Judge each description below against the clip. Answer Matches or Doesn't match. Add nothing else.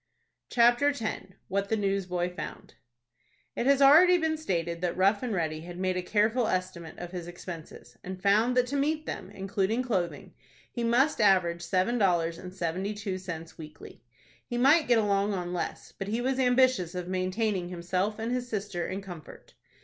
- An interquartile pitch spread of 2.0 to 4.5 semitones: Doesn't match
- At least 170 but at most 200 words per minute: Matches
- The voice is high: Matches